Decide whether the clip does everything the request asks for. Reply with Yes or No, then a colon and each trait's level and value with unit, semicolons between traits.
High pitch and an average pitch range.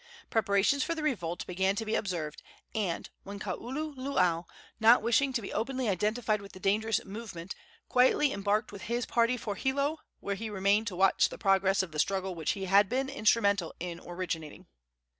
Yes: high, 205 Hz; average, 3.8 semitones